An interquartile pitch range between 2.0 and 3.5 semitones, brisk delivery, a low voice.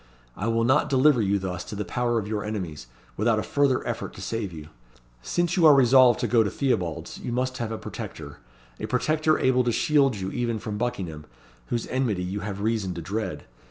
No: average, 4.4 semitones; fast, 210 wpm; low, 115 Hz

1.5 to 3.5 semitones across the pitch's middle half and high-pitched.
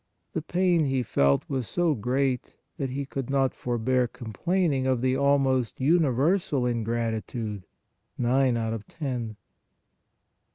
No: average, 3.0 semitones; low, 130 Hz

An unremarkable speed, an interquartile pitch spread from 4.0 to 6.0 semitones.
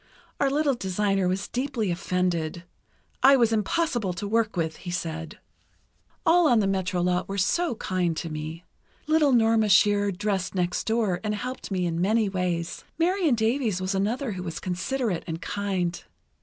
Yes: average, 165 wpm; average, 4.6 semitones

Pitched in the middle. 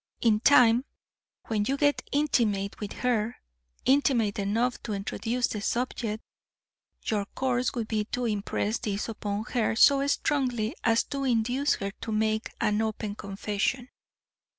No: high, 225 Hz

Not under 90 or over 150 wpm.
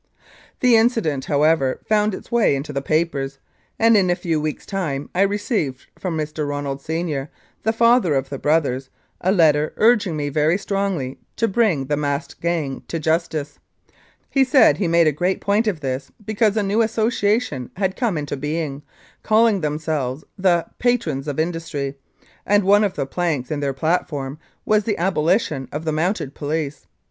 No: average, 175 wpm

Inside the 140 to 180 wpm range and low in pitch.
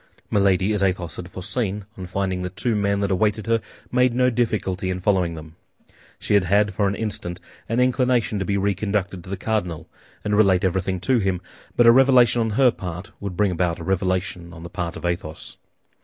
No: average, 200 wpm; low, 100 Hz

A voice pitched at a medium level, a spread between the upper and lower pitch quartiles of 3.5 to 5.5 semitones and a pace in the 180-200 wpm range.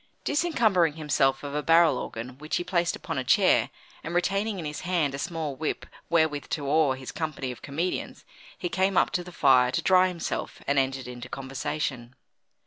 Yes: medium, 150 Hz; average, 4.7 semitones; average, 190 wpm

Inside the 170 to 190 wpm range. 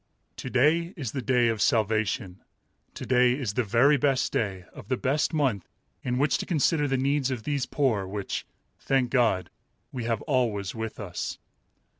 Yes: average, 175 wpm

